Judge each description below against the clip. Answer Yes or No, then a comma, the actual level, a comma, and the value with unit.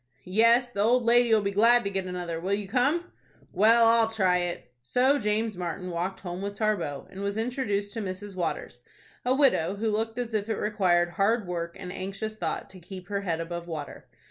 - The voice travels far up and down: No, average, 3.9 semitones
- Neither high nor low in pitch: No, high, 200 Hz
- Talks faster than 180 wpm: Yes, average, 195 wpm